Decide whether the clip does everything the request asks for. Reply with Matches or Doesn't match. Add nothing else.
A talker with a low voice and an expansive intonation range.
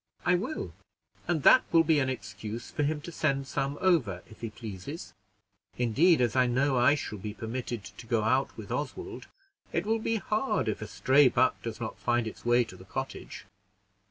Matches